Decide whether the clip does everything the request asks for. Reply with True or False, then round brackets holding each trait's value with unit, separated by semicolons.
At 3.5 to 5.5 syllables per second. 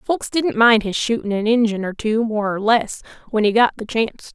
True (5.1 syllables/s)